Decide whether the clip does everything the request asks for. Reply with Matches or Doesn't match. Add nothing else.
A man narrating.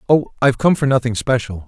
Matches